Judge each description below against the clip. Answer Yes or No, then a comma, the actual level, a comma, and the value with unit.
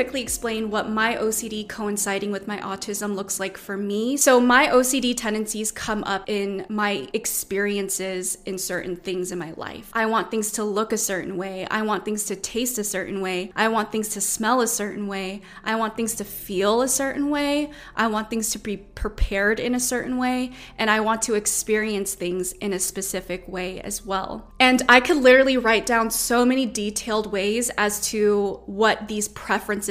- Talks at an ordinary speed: Yes, average, 195 wpm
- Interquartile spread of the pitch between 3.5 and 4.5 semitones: No, narrow, 2.4 semitones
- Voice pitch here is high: Yes, high, 210 Hz